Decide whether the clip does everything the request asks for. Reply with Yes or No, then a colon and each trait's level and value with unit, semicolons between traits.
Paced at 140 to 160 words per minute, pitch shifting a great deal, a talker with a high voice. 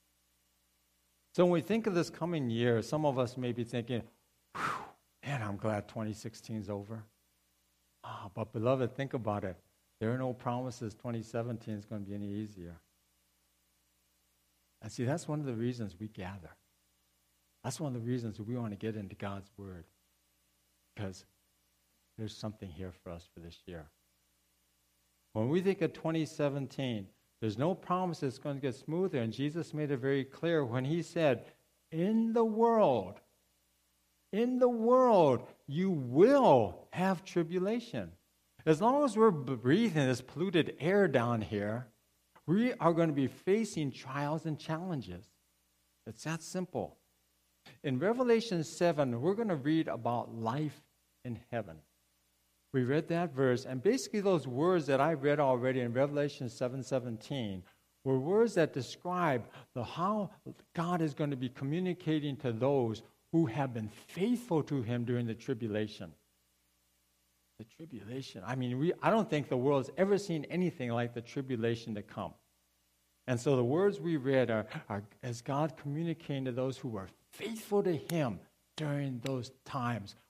No: average, 155 wpm; wide, 7.9 semitones; low, 125 Hz